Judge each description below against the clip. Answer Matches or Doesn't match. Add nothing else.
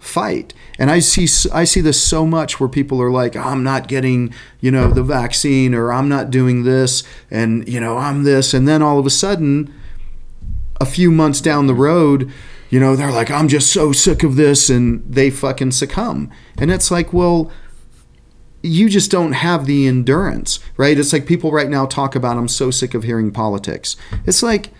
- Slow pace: Doesn't match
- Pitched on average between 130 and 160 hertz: Matches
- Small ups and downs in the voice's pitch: Doesn't match